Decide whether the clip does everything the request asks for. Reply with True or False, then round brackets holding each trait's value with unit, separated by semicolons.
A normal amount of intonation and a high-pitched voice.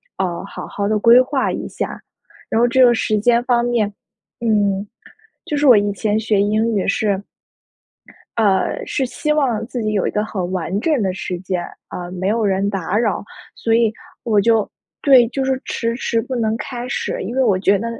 True (3.2 semitones; 220 Hz)